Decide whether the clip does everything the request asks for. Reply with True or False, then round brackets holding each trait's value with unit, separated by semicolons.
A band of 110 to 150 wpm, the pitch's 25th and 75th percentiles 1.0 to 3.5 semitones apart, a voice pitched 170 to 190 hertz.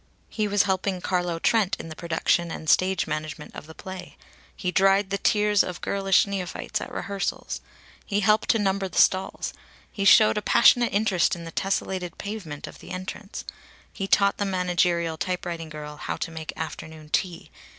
False (175 wpm; 3.1 semitones; 185 Hz)